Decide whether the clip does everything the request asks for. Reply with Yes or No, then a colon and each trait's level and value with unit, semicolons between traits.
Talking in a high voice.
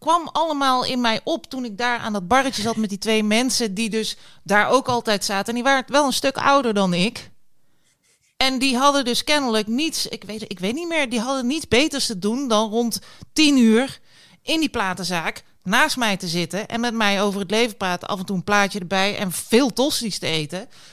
Yes: high, 230 Hz